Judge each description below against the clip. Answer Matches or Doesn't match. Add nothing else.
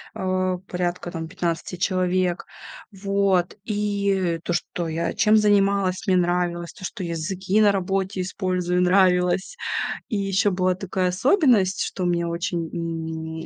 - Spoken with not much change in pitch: Matches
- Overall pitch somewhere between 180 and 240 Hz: Matches